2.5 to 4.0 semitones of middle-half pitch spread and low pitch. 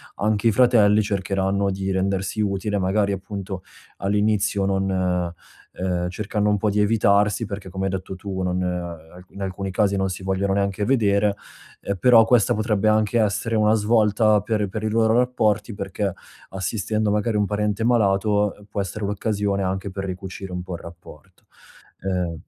No: narrow, 1.9 semitones; low, 100 Hz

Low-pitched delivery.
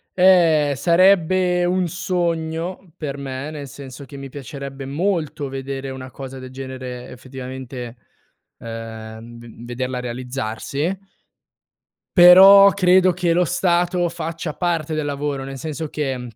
No: medium, 145 Hz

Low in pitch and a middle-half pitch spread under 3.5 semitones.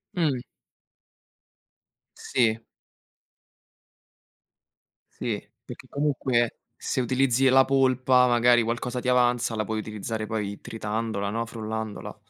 Yes: low, 120 Hz; narrow, 2.5 semitones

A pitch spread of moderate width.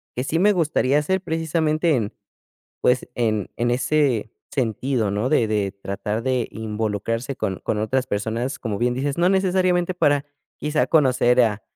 No: wide, 5.7 semitones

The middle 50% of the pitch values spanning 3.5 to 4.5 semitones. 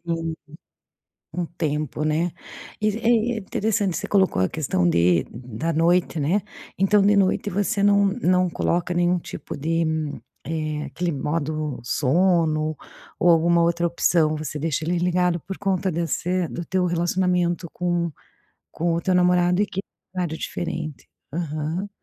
No: average, 2.8 semitones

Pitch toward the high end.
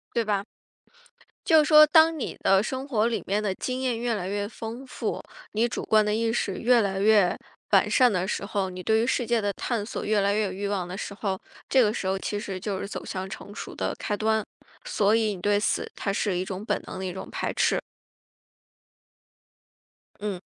Yes: high, 210 Hz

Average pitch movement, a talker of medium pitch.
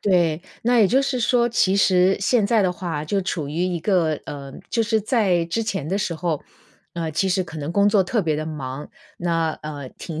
Yes: average, 4.6 semitones; medium, 180 Hz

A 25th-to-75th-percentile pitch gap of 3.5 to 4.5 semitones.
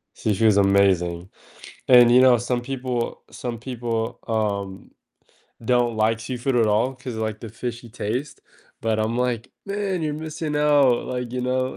No: average, 2.8 semitones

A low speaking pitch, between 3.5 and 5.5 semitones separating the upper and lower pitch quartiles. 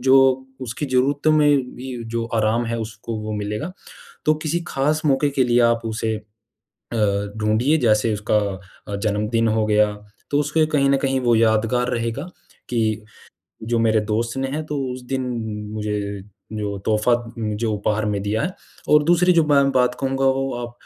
Yes: low, 115 Hz; average, 4.2 semitones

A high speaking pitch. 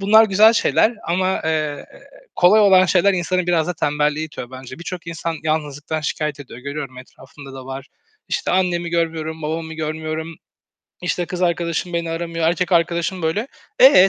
No: medium, 165 Hz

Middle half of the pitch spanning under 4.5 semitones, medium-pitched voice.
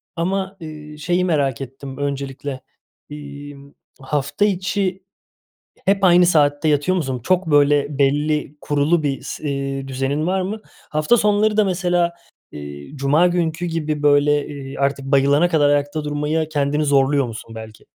Yes: average, 3.8 semitones; medium, 150 Hz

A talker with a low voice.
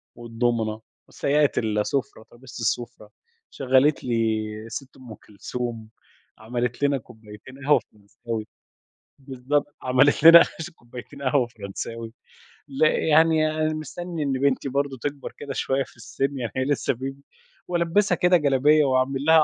Yes: low, 130 Hz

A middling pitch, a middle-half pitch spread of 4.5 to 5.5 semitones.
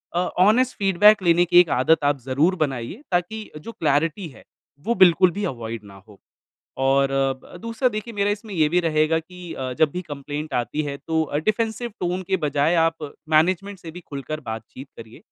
Yes: medium, 165 Hz; average, 5.0 semitones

